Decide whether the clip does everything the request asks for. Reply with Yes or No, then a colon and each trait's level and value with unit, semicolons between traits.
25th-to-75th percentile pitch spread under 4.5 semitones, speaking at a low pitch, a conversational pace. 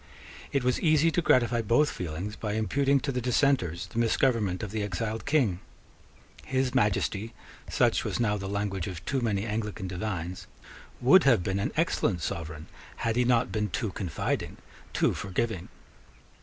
No: average, 4.8 semitones; low, 110 Hz; average, 160 wpm